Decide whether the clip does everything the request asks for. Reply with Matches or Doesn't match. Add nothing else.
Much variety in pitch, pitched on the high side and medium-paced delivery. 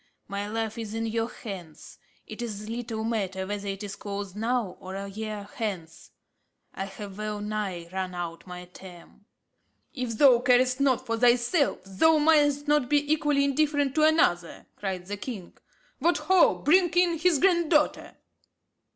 Matches